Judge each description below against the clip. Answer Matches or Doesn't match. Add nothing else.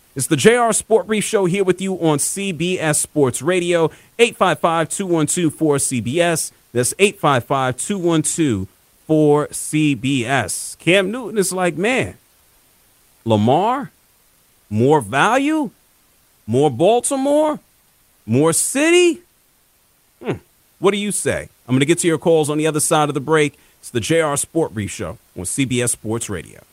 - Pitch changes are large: Matches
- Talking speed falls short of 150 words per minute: Matches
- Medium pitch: Matches